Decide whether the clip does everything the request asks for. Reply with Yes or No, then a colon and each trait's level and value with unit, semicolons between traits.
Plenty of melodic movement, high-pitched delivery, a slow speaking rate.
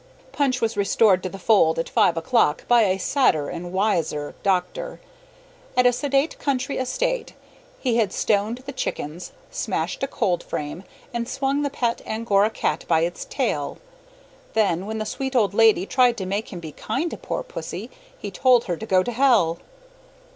No: wide, 5.9 semitones; high, 220 Hz; average, 175 wpm